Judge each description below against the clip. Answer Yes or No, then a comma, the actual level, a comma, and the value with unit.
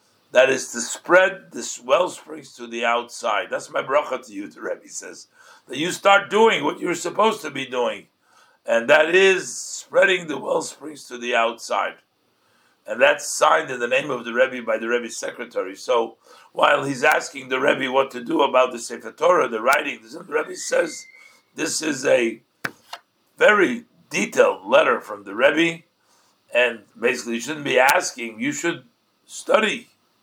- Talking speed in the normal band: Yes, average, 170 wpm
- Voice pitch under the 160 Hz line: No, medium, 170 Hz